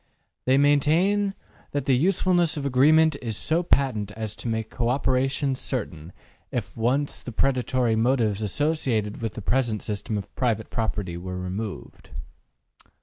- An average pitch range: Yes, average, 4.7 semitones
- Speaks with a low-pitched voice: Yes, low, 125 Hz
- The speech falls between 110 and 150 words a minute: Yes, average, 145 wpm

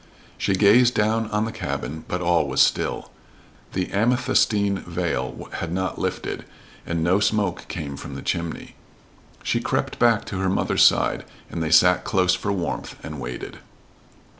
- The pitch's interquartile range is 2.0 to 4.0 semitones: Yes, average, 3.7 semitones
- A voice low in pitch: Yes, very low, 95 Hz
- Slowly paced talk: No, average, 160 wpm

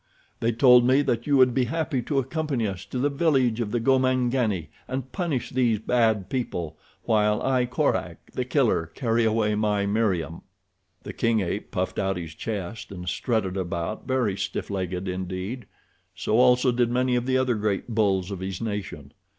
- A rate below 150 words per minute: No, average, 175 wpm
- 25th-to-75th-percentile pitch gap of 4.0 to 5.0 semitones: Yes, average, 4.5 semitones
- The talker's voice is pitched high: No, low, 115 Hz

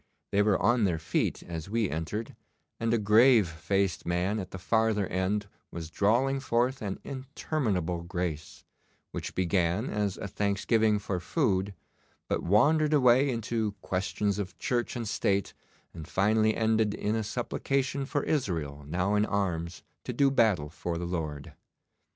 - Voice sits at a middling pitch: No, low, 105 Hz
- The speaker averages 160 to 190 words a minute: No, average, 150 wpm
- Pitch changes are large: No, average, 4.4 semitones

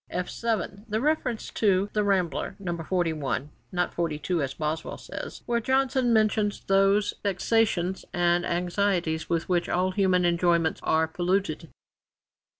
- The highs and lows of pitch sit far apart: No, average, 3.3 semitones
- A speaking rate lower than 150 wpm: Yes, average, 140 wpm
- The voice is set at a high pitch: No, medium, 180 Hz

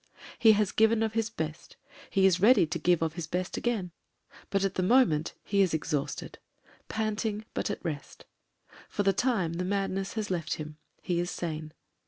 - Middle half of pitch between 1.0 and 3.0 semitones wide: No, average, 4.6 semitones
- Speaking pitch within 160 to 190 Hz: Yes, medium, 185 Hz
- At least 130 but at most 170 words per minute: No, average, 185 wpm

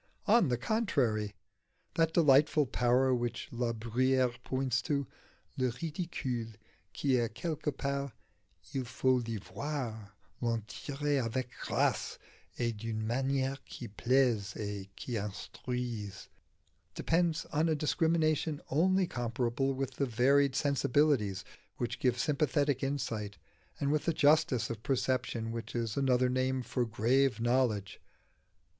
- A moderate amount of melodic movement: Yes, average, 3.4 semitones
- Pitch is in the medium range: No, low, 130 Hz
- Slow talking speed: Yes, slow, 125 wpm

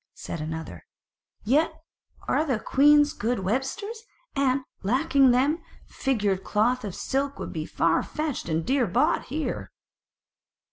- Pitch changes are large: Yes, wide, 5.8 semitones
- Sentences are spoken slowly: Yes, slow, 130 wpm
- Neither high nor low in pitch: No, very high, 260 Hz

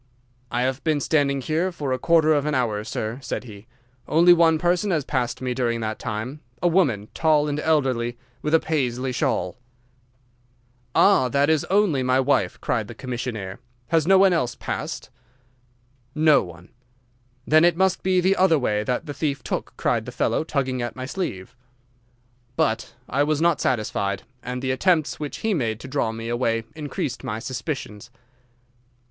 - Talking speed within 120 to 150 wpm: No, average, 170 wpm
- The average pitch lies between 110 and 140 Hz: Yes, low, 135 Hz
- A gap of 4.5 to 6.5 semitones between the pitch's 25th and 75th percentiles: Yes, average, 4.9 semitones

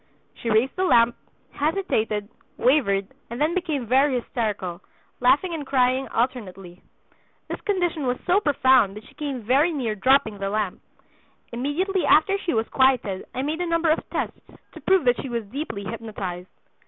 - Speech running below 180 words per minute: Yes, average, 165 wpm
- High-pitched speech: Yes, very high, 255 Hz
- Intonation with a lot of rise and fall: Yes, wide, 5.9 semitones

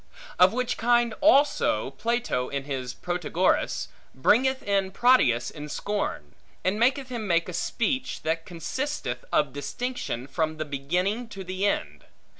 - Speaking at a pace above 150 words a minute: No, average, 140 wpm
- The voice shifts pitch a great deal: Yes, wide, 8.6 semitones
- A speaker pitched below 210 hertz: Yes, high, 190 Hz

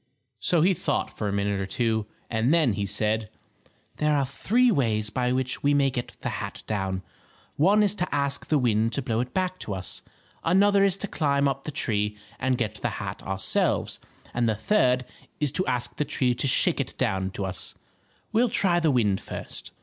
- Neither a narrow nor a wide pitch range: No, wide, 6.4 semitones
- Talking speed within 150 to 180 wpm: No, fast, 205 wpm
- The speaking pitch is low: Yes, low, 125 Hz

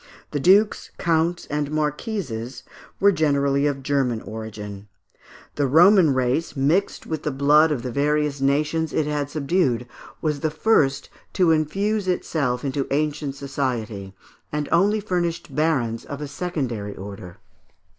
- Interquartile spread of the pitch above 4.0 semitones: No, average, 3.5 semitones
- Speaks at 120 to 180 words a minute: Yes, slow, 135 wpm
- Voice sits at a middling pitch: Yes, medium, 145 Hz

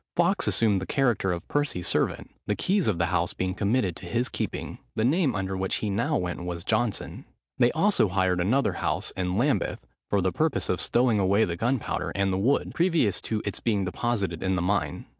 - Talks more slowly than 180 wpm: No, fast, 205 wpm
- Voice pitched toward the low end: Yes, low, 100 Hz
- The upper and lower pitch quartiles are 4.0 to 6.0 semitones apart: Yes, average, 4.7 semitones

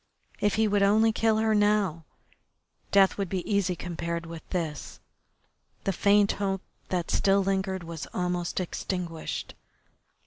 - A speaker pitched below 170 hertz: No, high, 190 Hz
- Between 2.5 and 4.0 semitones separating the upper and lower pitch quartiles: Yes, average, 2.9 semitones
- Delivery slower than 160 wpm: Yes, slow, 135 wpm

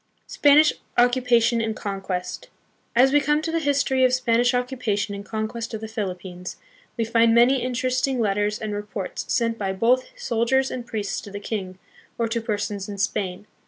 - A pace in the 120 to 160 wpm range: No, average, 170 wpm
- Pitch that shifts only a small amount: No, average, 3.6 semitones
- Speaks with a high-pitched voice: Yes, high, 230 Hz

